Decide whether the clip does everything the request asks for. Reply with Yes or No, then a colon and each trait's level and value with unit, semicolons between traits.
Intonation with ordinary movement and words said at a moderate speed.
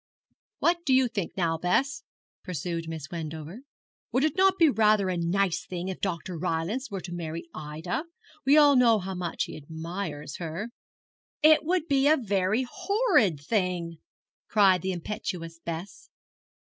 No: wide, 7.5 semitones; average, 155 wpm